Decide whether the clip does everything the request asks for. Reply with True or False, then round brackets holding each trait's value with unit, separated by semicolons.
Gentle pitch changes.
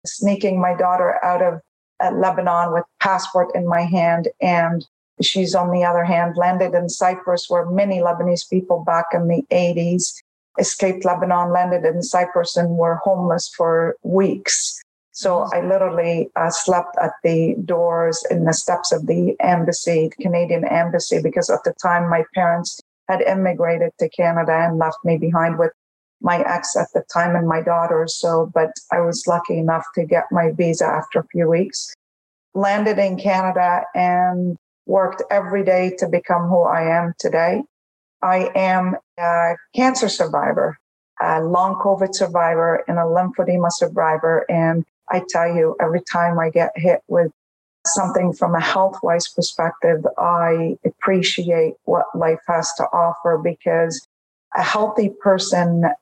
True (1.6 semitones)